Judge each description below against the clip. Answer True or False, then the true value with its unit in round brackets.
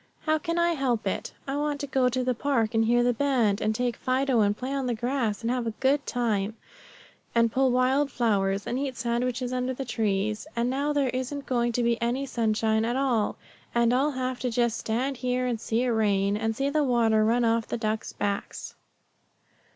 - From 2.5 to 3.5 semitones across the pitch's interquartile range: True (2.8 semitones)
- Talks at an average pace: False (215 wpm)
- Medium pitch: False (245 Hz)